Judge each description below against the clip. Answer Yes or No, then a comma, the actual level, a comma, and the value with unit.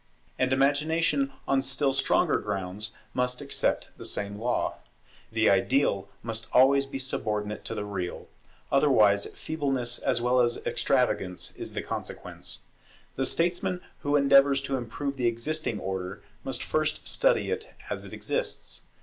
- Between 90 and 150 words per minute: Yes, average, 140 wpm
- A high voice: No, low, 130 Hz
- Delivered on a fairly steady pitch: No, average, 4.7 semitones